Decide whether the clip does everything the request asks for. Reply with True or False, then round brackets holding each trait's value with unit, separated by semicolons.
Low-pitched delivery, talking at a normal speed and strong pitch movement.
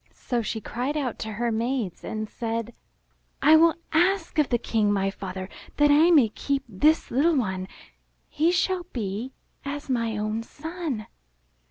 False (245 Hz; 165 wpm; 5.9 semitones)